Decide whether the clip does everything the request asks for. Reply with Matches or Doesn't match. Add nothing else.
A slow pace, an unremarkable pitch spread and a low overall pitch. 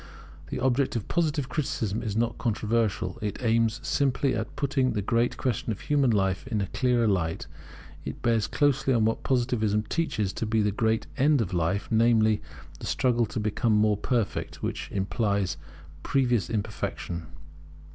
Doesn't match